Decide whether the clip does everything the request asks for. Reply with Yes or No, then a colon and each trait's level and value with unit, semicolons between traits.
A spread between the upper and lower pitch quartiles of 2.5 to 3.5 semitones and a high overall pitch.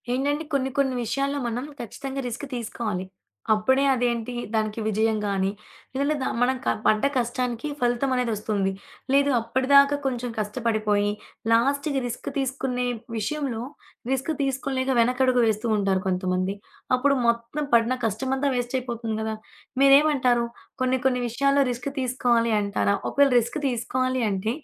Yes: average, 3.1 semitones; high, 245 Hz